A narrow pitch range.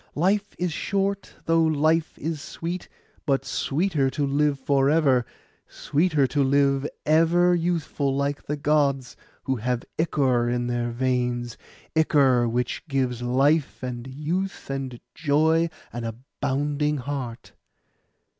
No: average, 3.7 semitones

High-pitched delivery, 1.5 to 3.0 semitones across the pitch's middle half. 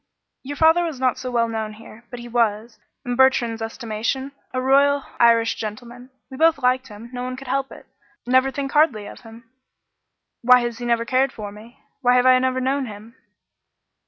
Yes: very high, 250 Hz; narrow, 2.4 semitones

